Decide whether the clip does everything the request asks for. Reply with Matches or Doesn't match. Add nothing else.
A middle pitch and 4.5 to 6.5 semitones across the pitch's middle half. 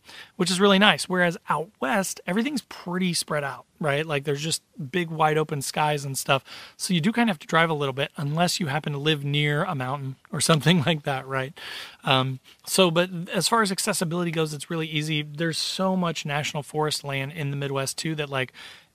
Doesn't match